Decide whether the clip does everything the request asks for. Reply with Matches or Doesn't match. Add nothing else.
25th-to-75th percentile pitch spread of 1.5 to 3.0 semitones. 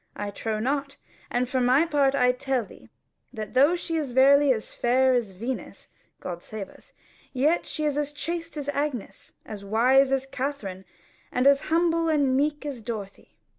Doesn't match